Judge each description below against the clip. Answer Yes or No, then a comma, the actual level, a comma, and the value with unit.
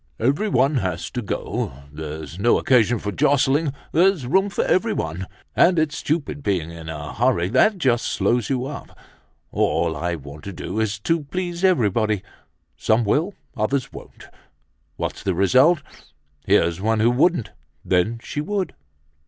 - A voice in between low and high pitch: No, low, 120 Hz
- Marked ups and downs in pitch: Yes, wide, 8.1 semitones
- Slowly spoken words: No, average, 150 wpm